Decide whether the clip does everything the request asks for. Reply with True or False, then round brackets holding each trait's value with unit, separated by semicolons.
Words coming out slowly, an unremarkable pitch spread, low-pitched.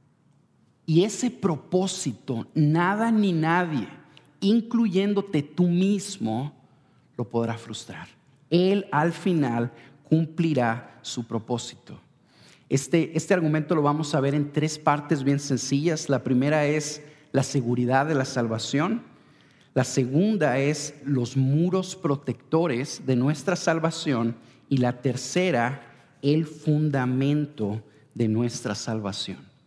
False (110 wpm; 4.5 semitones; 145 Hz)